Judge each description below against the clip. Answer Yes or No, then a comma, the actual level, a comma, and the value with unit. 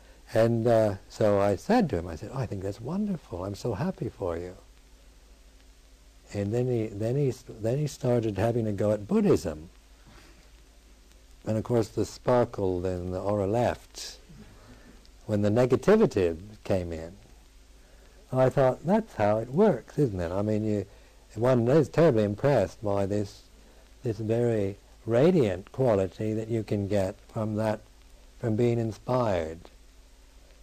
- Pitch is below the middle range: Yes, low, 105 Hz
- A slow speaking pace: No, average, 150 wpm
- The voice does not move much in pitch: No, average, 4.9 semitones